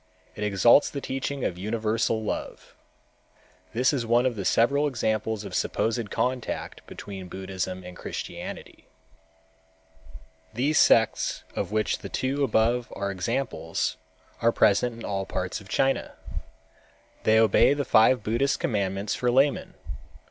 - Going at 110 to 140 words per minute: Yes, slow, 135 wpm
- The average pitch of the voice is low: Yes, low, 115 Hz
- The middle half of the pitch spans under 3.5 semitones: No, average, 4.2 semitones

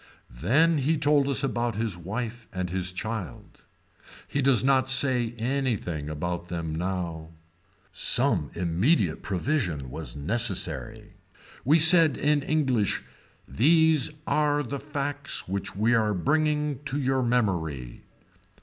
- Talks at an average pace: No, slow, 120 wpm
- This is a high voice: No, low, 120 Hz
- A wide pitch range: Yes, wide, 7.9 semitones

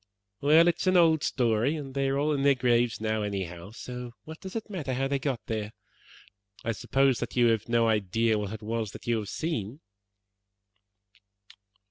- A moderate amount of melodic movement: Yes, average, 4.3 semitones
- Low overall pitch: Yes, low, 120 Hz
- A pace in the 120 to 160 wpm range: No, average, 190 wpm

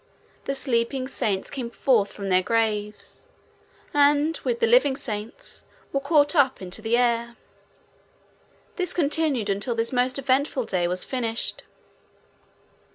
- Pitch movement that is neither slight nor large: Yes, average, 4.3 semitones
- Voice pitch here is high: Yes, very high, 250 Hz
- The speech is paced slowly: Yes, slow, 130 wpm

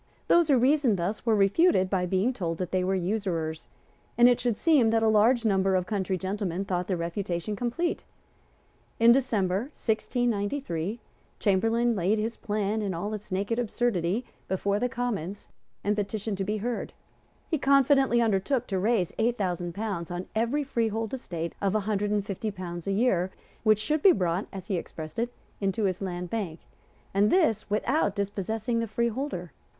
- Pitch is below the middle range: No, high, 210 Hz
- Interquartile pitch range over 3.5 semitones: Yes, average, 3.9 semitones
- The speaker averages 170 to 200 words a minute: Yes, average, 175 wpm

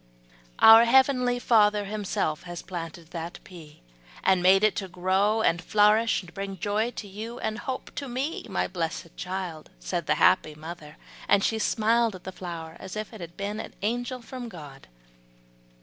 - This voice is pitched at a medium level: No, high, 200 Hz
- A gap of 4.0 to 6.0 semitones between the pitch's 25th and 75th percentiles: Yes, average, 4.5 semitones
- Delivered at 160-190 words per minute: Yes, average, 170 wpm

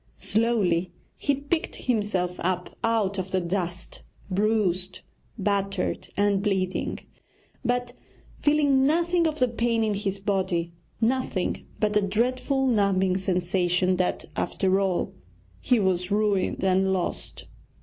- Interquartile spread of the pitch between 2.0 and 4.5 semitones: Yes, average, 3.9 semitones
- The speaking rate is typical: No, slow, 120 wpm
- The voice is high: Yes, high, 200 Hz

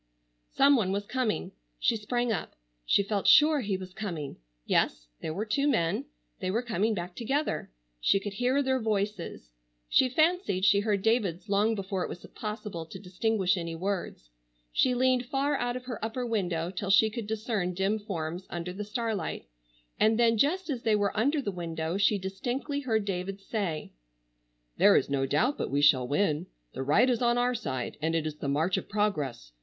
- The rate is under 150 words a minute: No, average, 190 wpm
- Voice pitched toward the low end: No, high, 205 Hz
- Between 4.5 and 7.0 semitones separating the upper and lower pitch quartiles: Yes, average, 5.2 semitones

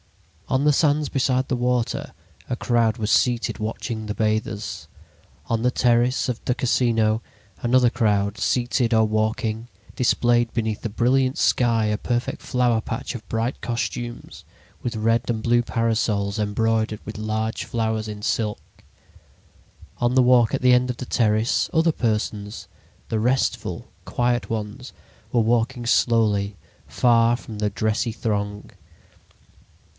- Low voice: Yes, low, 115 Hz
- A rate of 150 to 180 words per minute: No, average, 140 wpm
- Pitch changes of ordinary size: No, narrow, 2.2 semitones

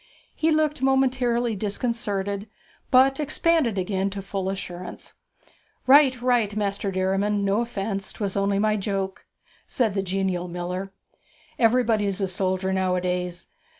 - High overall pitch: Yes, high, 200 Hz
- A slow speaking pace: Yes, slow, 120 wpm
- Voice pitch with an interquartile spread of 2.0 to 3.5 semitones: No, average, 3.9 semitones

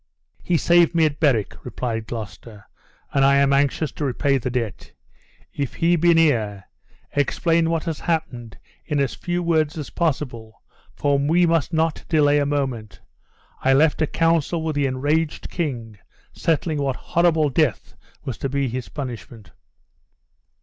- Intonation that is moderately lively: Yes, average, 4.4 semitones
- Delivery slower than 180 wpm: Yes, average, 155 wpm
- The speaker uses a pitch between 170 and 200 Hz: No, medium, 145 Hz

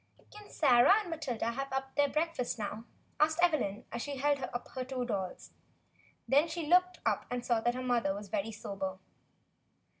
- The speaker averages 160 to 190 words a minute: Yes, average, 175 wpm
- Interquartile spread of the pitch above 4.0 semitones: Yes, average, 5.1 semitones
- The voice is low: No, very high, 255 Hz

